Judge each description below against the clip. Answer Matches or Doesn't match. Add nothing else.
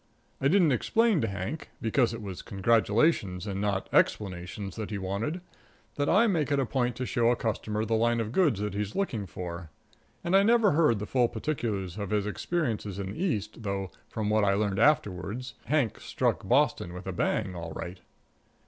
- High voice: Doesn't match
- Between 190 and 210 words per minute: Matches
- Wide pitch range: Matches